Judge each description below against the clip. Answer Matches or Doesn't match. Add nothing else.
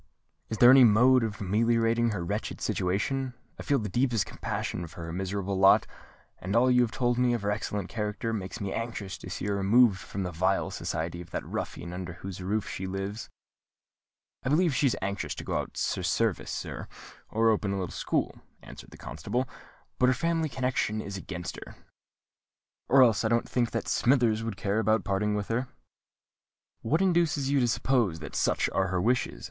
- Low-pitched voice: Matches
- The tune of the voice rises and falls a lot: Doesn't match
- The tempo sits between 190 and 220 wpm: Matches